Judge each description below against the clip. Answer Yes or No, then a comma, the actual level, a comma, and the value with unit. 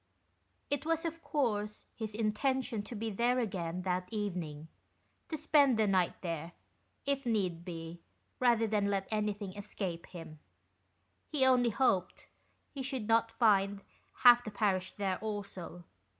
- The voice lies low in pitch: No, high, 210 Hz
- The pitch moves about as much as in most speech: Yes, average, 4.7 semitones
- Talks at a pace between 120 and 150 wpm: Yes, average, 140 wpm